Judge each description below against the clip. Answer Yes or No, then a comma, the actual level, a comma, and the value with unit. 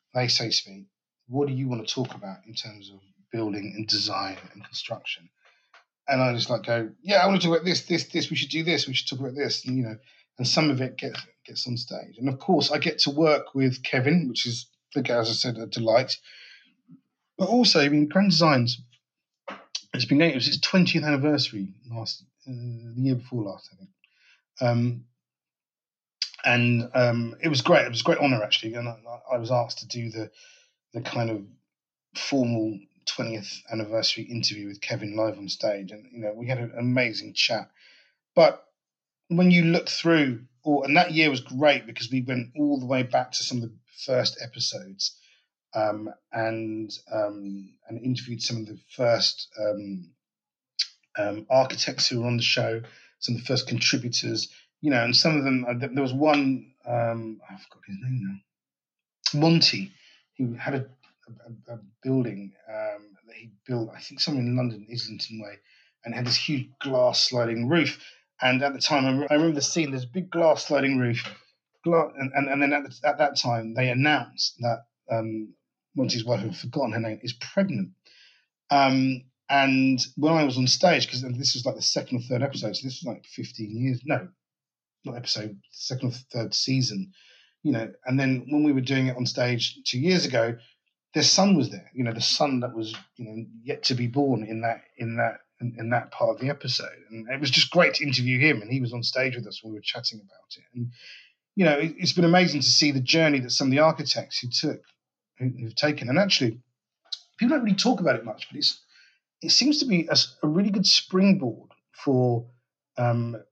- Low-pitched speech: Yes, low, 125 Hz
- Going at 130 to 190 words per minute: No, fast, 205 wpm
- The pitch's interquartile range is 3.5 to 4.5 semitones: Yes, average, 4.1 semitones